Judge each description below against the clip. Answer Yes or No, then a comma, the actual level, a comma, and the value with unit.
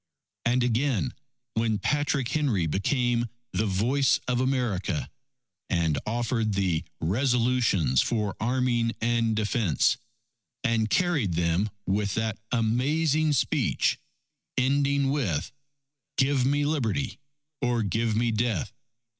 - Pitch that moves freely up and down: No, average, 3.8 semitones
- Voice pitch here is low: Yes, low, 115 Hz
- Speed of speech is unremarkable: No, slow, 105 wpm